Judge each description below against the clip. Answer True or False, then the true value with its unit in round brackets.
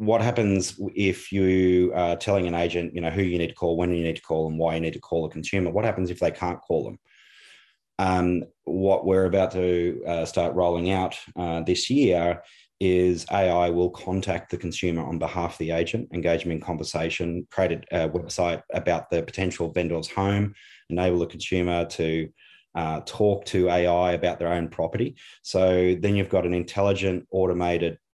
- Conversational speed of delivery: True (190 wpm)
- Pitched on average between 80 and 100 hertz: True (90 Hz)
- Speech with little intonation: True (1.8 semitones)